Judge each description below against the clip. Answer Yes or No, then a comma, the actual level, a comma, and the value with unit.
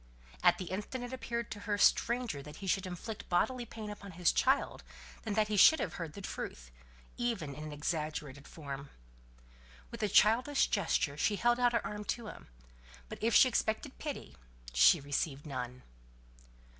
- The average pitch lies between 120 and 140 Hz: No, high, 200 Hz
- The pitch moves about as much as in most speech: No, wide, 7.6 semitones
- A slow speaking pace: No, average, 175 wpm